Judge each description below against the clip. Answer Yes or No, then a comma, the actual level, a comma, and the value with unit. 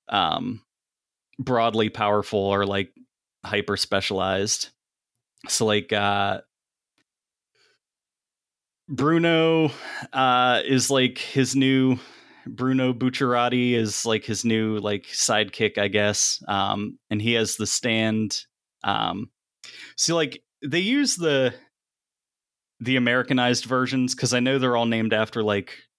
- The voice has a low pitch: Yes, low, 120 Hz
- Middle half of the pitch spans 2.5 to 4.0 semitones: Yes, average, 3.7 semitones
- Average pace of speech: No, slow, 115 wpm